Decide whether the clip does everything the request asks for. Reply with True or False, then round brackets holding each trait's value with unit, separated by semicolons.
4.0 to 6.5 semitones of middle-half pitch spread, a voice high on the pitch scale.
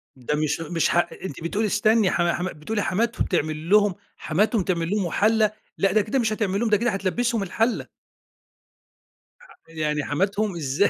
True (4.5 semitones; 195 Hz)